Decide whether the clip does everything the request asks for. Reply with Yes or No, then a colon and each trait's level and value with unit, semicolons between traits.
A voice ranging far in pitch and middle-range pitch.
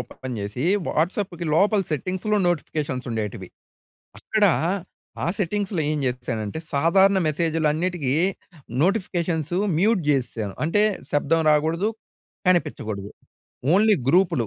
Yes: wide, 5.8 semitones; medium, 165 Hz